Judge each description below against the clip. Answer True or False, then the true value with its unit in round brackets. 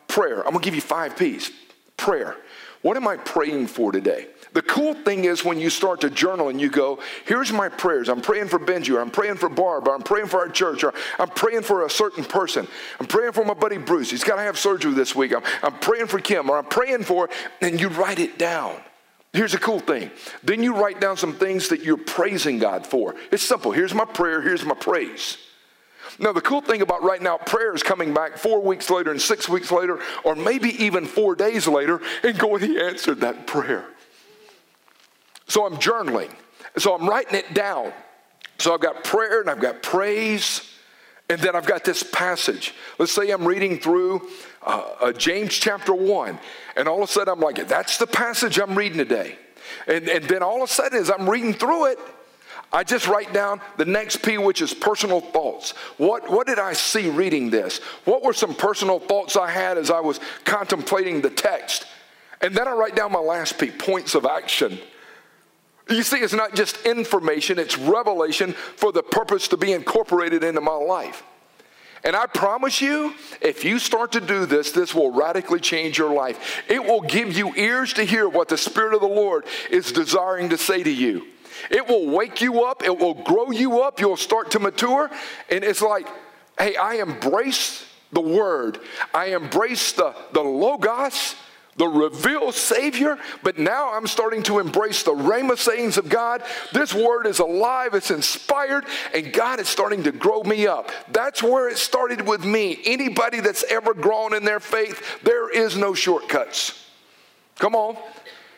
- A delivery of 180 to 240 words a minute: True (195 wpm)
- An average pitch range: False (5.7 semitones)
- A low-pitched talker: False (215 Hz)